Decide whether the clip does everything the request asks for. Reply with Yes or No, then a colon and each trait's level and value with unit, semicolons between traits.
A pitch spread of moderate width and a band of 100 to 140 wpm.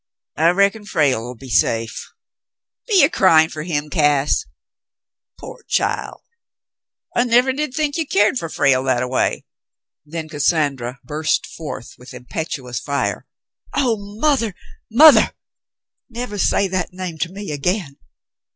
No: wide, 7.7 semitones; slow, 135 wpm